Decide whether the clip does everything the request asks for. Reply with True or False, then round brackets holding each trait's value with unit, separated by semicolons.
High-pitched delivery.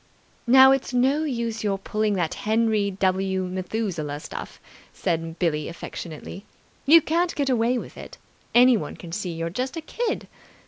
True (215 Hz)